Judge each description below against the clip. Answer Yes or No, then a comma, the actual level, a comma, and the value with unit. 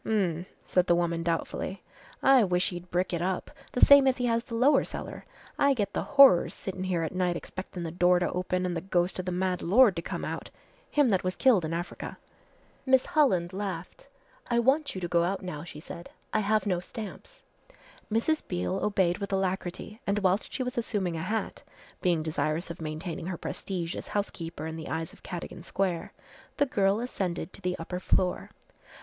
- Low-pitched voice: No, medium, 185 Hz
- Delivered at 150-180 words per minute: No, average, 200 wpm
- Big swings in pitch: No, average, 3.6 semitones